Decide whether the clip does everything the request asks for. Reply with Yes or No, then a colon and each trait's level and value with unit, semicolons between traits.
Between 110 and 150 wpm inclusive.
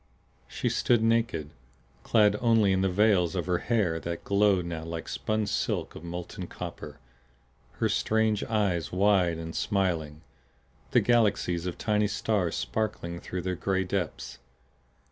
Yes: average, 145 wpm